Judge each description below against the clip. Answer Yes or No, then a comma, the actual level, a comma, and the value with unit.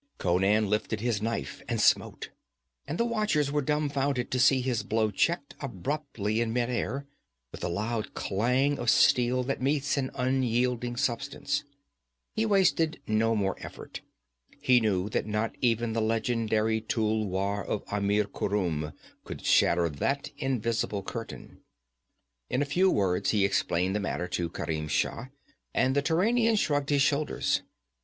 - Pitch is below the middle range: Yes, low, 115 Hz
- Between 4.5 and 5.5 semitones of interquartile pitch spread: Yes, average, 5.0 semitones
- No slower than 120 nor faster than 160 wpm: Yes, average, 145 wpm